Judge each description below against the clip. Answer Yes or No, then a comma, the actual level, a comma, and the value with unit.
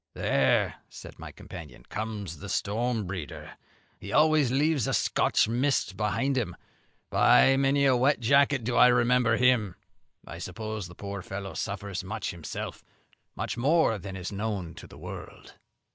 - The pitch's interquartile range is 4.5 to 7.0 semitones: Yes, average, 4.8 semitones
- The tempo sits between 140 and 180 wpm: Yes, average, 155 wpm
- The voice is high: No, low, 110 Hz